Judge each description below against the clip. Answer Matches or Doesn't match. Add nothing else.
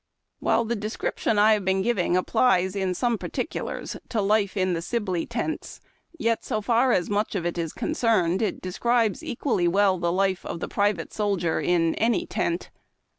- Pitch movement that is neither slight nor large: Matches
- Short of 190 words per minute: Matches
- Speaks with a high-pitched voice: Matches